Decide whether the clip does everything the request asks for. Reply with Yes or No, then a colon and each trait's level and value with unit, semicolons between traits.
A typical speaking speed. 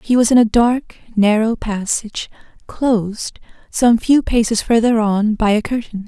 Yes: average, 160 wpm